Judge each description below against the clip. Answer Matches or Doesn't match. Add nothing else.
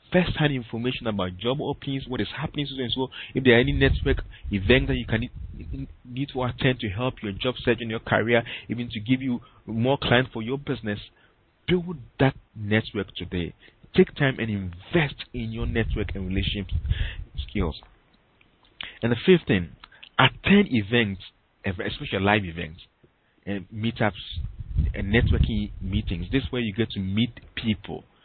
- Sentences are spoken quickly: Doesn't match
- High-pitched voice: Doesn't match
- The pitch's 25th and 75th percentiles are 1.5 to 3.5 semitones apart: Doesn't match